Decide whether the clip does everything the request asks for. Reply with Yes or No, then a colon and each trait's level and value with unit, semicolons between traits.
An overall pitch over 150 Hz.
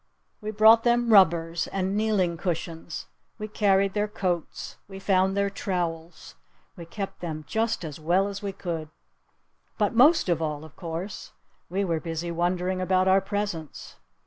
Yes: medium, 185 Hz